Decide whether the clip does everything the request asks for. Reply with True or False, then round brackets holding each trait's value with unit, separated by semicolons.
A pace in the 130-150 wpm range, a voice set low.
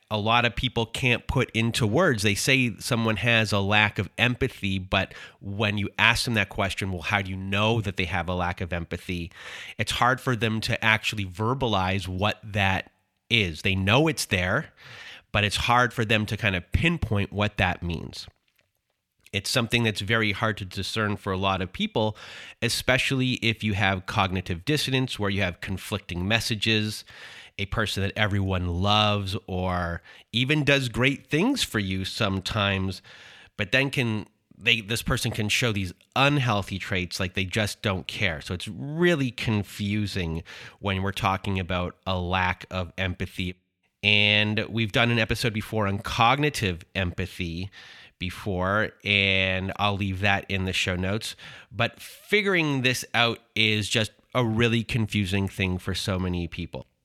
False (165 wpm; 105 Hz)